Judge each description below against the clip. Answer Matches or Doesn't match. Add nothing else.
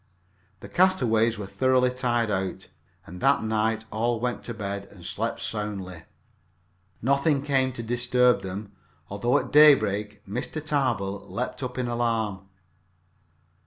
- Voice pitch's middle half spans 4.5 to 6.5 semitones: Doesn't match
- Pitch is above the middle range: Doesn't match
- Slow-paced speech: Matches